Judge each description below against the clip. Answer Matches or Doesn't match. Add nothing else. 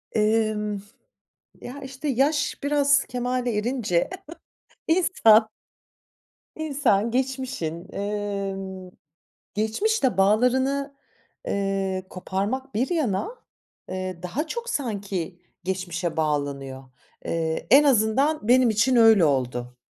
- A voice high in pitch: Matches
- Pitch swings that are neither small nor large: Doesn't match